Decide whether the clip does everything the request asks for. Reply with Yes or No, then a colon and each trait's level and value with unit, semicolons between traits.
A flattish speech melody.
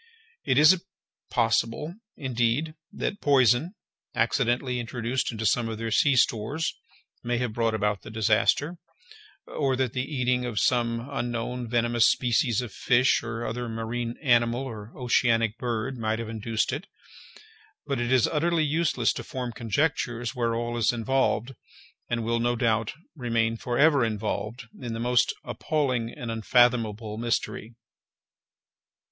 Yes: narrow, 2.2 semitones